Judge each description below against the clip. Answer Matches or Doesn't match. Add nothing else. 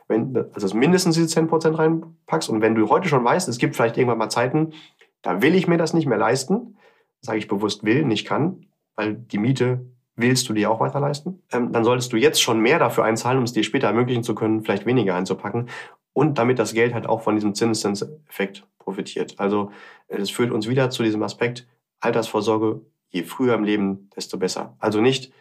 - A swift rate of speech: Matches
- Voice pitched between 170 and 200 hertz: Doesn't match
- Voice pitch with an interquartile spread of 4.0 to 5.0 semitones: Matches